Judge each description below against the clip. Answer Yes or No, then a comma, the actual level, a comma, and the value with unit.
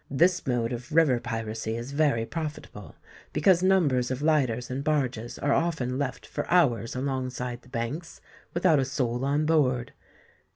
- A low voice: Yes, low, 130 Hz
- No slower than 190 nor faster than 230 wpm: No, average, 155 wpm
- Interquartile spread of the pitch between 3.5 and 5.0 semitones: Yes, average, 4.1 semitones